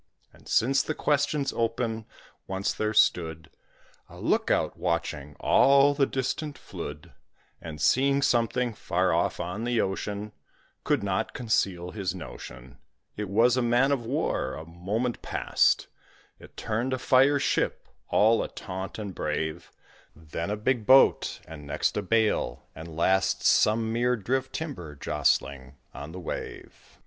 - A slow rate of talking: No, average, 145 wpm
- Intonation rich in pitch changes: Yes, wide, 6.9 semitones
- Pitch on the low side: Yes, low, 110 Hz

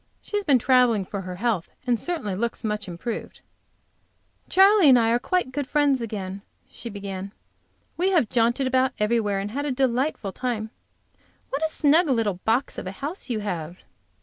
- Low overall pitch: No, high, 235 Hz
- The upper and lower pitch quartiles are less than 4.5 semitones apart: No, average, 5.1 semitones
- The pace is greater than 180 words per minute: No, average, 175 wpm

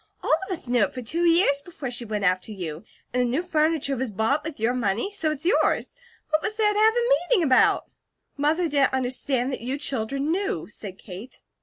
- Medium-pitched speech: No, very high, 275 Hz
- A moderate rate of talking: No, fast, 215 wpm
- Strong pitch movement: Yes, wide, 5.8 semitones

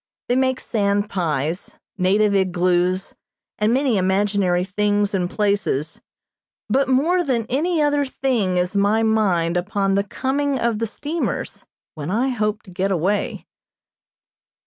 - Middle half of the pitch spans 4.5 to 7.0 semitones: Yes, average, 5.3 semitones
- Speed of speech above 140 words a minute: No, slow, 135 wpm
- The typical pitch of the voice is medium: No, high, 205 Hz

